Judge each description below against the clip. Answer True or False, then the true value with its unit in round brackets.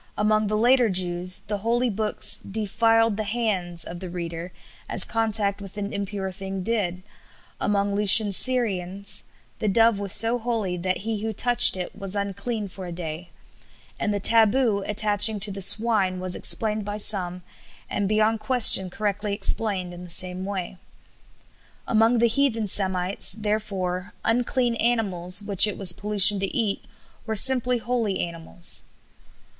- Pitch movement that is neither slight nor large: True (3.1 semitones)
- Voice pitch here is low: False (205 Hz)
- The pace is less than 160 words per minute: True (150 wpm)